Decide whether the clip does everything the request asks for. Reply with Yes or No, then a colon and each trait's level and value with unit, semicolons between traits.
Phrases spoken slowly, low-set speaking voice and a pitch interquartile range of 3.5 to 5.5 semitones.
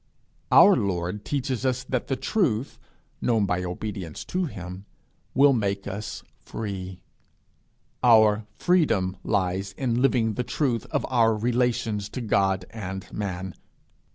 Yes: slow, 125 wpm; low, 110 Hz; average, 4.4 semitones